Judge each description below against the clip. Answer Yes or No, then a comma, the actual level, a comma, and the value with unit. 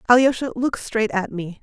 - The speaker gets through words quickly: No, average, 185 wpm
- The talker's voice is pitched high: Yes, high, 235 Hz